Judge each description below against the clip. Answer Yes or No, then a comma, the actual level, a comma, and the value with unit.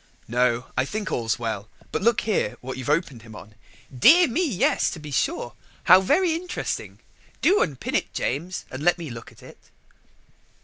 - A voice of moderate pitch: Yes, medium, 150 Hz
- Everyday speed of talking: Yes, average, 180 wpm